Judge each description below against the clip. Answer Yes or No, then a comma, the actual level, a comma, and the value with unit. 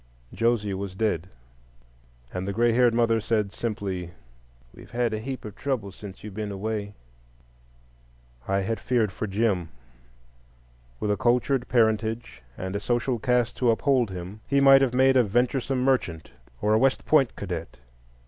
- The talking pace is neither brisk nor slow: Yes, average, 160 wpm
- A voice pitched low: Yes, low, 110 Hz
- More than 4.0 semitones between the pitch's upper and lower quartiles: No, average, 3.6 semitones